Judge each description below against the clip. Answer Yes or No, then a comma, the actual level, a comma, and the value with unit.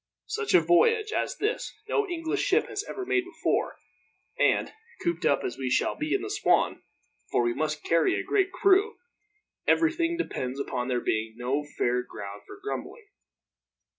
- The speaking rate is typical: Yes, average, 165 wpm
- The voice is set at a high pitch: Yes, very high, 330 Hz